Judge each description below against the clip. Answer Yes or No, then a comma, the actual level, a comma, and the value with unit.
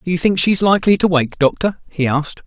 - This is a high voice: No, medium, 170 Hz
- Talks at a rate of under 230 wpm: No, fast, 270 wpm